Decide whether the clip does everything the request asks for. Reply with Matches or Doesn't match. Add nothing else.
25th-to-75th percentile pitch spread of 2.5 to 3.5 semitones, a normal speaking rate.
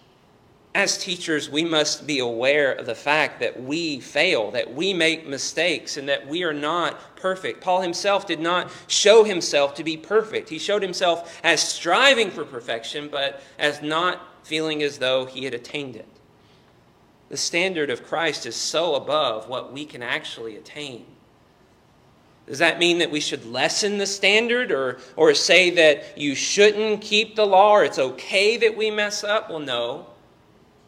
Doesn't match